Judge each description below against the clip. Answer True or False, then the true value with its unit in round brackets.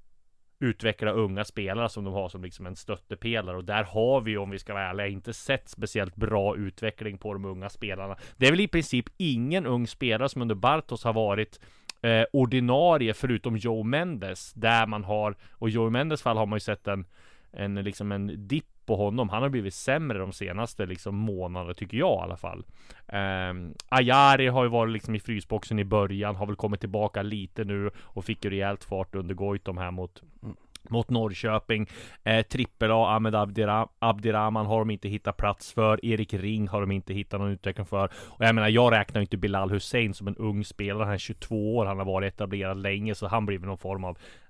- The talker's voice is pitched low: True (105 Hz)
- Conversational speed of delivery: False (200 wpm)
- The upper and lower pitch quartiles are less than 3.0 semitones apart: True (2.4 semitones)